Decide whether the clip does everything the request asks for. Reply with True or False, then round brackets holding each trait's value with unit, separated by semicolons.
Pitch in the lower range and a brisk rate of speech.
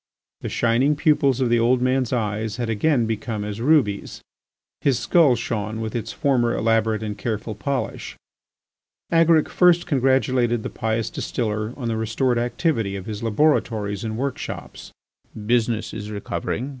False (115 Hz; 145 wpm)